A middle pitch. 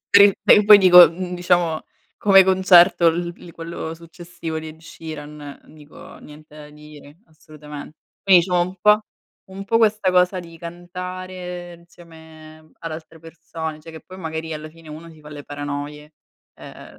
Yes: medium, 165 Hz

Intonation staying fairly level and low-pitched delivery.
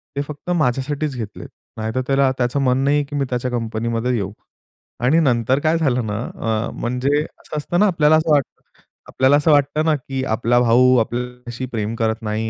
No: average, 3.7 semitones; low, 125 Hz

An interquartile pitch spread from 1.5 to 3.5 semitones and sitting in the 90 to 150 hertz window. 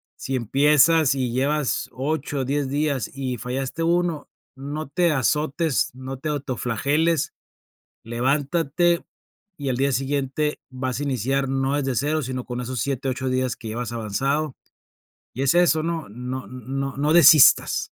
Yes: average, 2.7 semitones; low, 135 Hz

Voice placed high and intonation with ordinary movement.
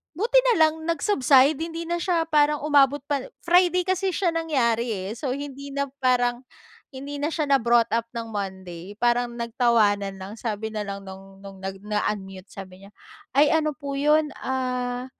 No: very high, 255 Hz; wide, 6.4 semitones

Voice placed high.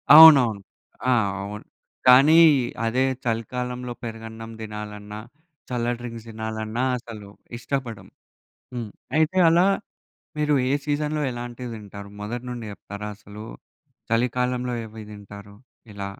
No: low, 115 Hz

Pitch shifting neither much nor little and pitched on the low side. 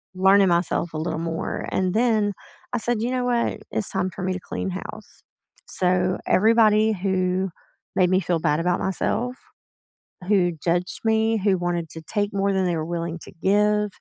No: average, 3.1 semitones; high, 190 Hz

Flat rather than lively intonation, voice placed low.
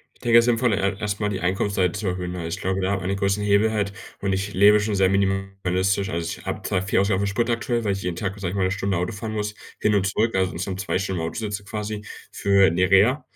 Yes: narrow, 1.8 semitones; low, 100 Hz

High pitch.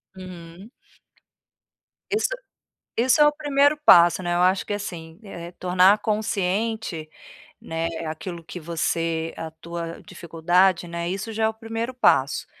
No: medium, 180 Hz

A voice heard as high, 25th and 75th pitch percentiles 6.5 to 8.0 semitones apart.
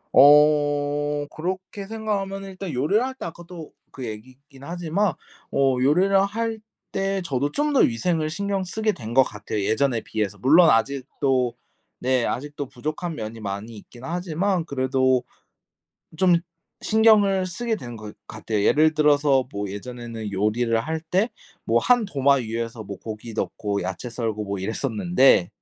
No: medium, 145 Hz; wide, 7.5 semitones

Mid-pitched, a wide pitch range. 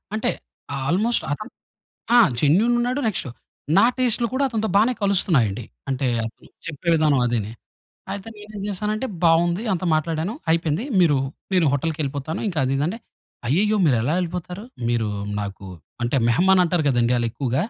Yes: medium, 165 Hz; wide, 7.2 semitones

